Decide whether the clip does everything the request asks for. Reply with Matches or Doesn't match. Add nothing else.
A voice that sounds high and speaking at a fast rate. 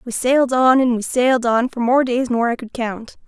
Matches